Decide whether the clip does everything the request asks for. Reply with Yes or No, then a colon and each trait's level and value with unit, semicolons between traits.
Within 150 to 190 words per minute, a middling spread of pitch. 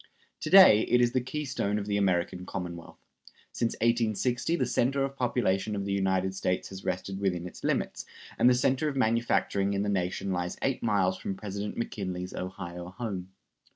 Yes: average, 180 wpm; average, 4.5 semitones